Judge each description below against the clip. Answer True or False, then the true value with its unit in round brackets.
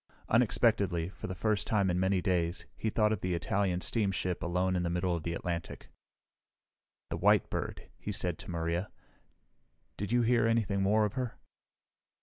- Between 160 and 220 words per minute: True (170 wpm)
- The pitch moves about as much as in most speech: True (3.4 semitones)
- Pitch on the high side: False (95 Hz)